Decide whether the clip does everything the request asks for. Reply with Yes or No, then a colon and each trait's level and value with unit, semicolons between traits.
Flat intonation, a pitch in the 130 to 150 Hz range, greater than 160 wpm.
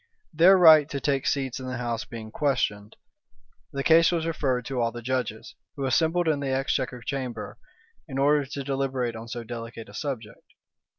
No: average, 3.4 semitones; low, 135 Hz; average, 180 wpm